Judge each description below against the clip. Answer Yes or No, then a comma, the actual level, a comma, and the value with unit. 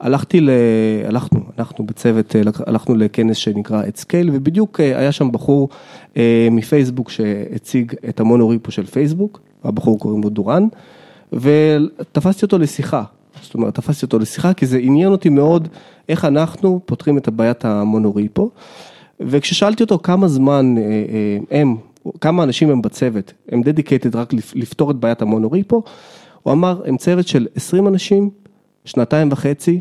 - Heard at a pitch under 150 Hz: Yes, medium, 140 Hz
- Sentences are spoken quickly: No, average, 135 wpm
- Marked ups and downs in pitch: Yes, wide, 6.6 semitones